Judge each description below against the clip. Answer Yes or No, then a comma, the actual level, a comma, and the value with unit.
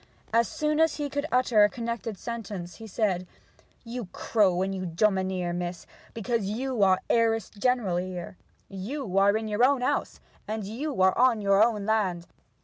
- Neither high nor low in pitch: No, high, 215 Hz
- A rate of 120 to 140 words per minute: No, average, 165 wpm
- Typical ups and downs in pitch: Yes, average, 3.8 semitones